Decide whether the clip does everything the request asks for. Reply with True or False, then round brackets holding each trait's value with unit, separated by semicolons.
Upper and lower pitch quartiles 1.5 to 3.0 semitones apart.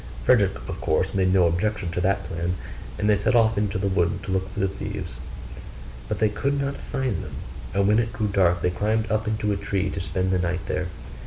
True (2.6 semitones)